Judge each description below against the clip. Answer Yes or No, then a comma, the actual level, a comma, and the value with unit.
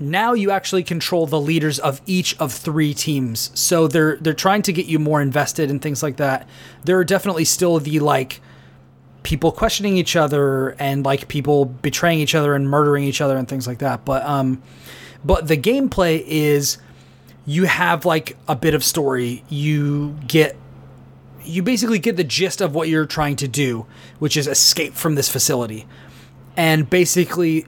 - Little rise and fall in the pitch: No, average, 3.6 semitones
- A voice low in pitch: No, medium, 150 Hz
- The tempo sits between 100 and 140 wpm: No, average, 180 wpm